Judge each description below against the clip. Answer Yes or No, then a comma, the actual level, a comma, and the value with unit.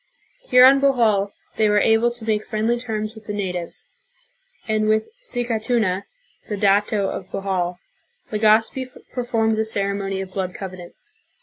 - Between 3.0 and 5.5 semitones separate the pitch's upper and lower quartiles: No, narrow, 2.5 semitones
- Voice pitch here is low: No, high, 215 Hz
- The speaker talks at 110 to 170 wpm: Yes, average, 140 wpm